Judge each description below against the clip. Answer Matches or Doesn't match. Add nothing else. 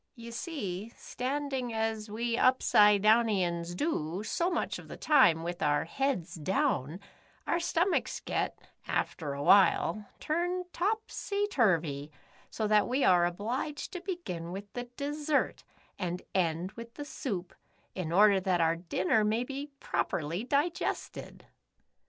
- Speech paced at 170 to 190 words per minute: Doesn't match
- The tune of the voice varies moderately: Doesn't match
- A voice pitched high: Matches